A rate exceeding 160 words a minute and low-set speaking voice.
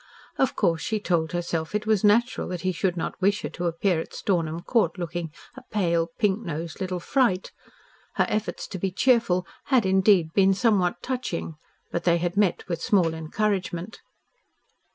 No: average, 175 wpm; medium, 185 Hz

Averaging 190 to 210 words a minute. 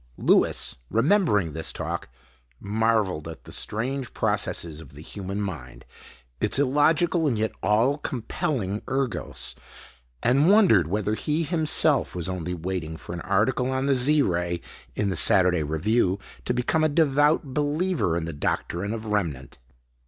No: average, 145 wpm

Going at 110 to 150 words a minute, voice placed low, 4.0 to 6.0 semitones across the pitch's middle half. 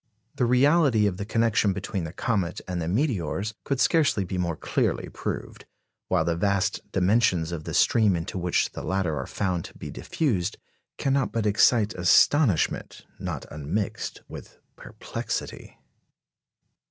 Yes: average, 145 wpm; low, 100 Hz; average, 4.7 semitones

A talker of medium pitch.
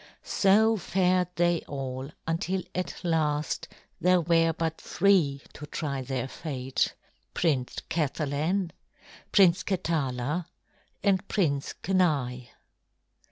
Yes: medium, 165 Hz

